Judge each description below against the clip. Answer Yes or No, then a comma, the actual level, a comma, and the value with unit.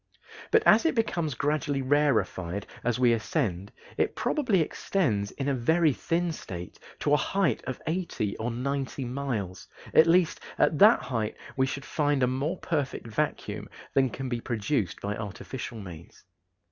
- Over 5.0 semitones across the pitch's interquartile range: Yes, wide, 5.5 semitones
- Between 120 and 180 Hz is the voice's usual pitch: Yes, low, 135 Hz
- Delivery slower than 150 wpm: No, average, 160 wpm